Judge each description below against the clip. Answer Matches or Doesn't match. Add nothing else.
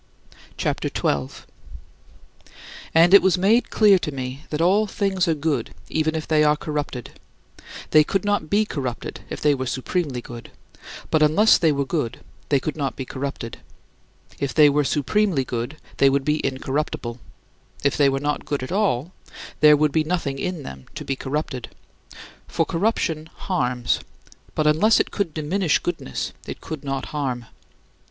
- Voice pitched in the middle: Matches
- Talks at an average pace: Matches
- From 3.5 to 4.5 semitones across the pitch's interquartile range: Matches